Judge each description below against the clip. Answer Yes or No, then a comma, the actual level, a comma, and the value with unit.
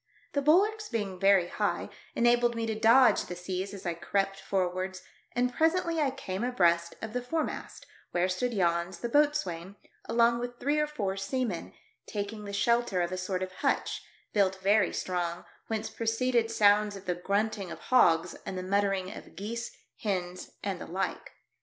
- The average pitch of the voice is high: Yes, high, 200 Hz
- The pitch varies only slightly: No, average, 4.4 semitones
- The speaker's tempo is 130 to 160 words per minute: No, average, 175 wpm